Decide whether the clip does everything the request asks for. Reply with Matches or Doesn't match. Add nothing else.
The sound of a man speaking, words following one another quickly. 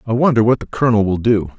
Matches